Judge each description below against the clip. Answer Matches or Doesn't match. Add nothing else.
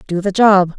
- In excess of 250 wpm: Doesn't match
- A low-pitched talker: Doesn't match